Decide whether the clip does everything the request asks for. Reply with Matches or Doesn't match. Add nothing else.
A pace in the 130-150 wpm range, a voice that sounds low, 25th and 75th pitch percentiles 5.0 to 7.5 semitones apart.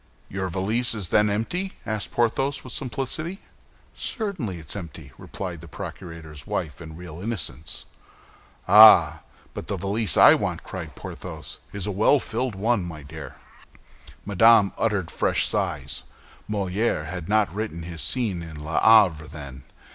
Matches